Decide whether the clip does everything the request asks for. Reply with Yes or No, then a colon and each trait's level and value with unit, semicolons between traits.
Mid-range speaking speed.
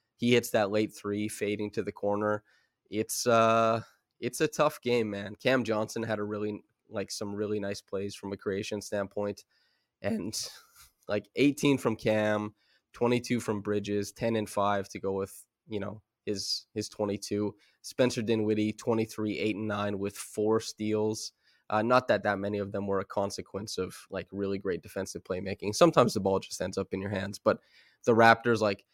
Yes: average, 180 wpm